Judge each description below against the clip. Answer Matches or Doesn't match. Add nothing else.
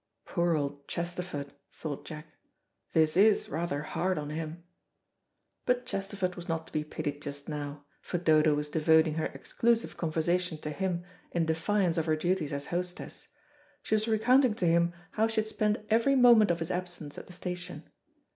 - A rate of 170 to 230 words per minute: Matches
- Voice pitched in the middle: Matches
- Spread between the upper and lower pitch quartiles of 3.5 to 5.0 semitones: Matches